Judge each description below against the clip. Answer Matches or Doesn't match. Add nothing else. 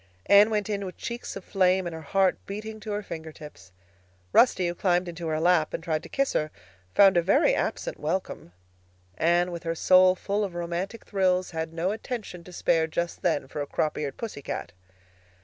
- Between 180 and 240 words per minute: Matches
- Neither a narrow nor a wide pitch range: Matches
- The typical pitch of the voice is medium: Matches